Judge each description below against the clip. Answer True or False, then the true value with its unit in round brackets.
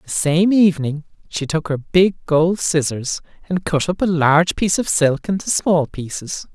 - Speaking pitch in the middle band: True (165 Hz)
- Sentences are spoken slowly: False (185 wpm)